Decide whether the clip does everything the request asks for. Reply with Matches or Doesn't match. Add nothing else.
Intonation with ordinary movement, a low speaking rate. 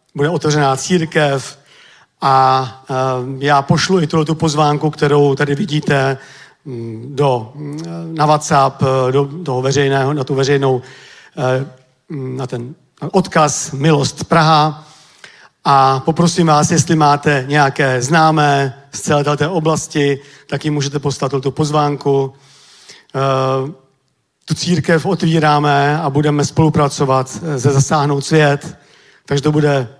Doesn't match